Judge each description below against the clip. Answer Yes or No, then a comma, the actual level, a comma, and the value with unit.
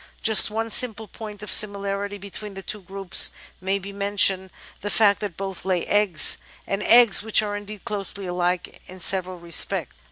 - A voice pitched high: Yes, high, 200 Hz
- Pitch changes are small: Yes, narrow, 1.8 semitones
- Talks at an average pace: Yes, average, 170 wpm